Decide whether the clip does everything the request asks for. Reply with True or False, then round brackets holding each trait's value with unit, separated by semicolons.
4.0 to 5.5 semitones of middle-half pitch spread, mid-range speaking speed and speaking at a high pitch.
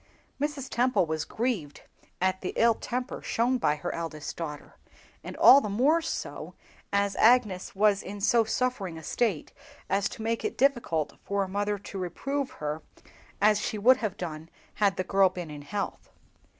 True (5.2 semitones; 175 wpm; 200 Hz)